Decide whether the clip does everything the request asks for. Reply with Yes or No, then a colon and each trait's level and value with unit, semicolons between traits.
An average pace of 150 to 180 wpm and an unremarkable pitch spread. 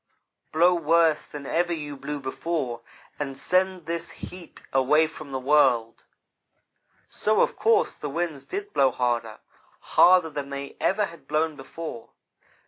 No: average, 140 wpm; average, 3.9 semitones